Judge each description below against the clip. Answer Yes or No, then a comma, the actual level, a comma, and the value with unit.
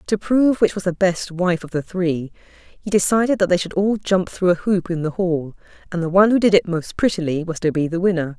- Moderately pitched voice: Yes, medium, 180 Hz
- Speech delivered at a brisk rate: Yes, fast, 255 wpm